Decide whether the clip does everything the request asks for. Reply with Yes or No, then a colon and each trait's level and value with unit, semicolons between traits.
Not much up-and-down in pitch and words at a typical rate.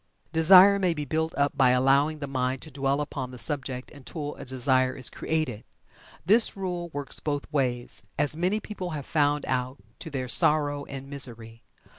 No: average, 3.4 semitones; average, 175 wpm